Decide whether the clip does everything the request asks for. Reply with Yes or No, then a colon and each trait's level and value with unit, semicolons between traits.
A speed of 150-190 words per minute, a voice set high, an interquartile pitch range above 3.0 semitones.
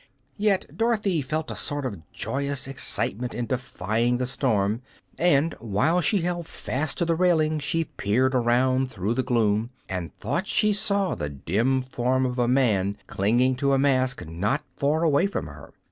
No: average, 170 wpm; low, 130 Hz; average, 5.1 semitones